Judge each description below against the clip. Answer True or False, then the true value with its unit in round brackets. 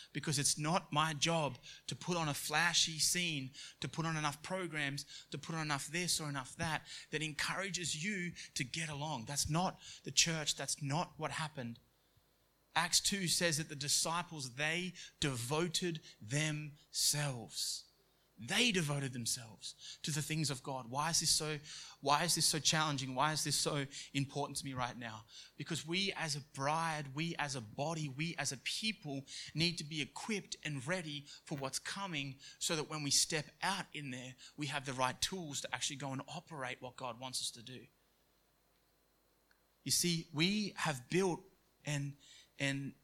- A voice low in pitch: False (150 Hz)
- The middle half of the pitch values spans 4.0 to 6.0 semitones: False (3.0 semitones)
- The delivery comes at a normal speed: True (175 wpm)